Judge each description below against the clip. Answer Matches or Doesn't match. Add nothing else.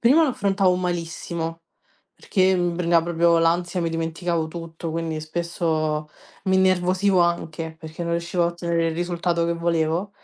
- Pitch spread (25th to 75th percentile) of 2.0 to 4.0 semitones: Doesn't match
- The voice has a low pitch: Doesn't match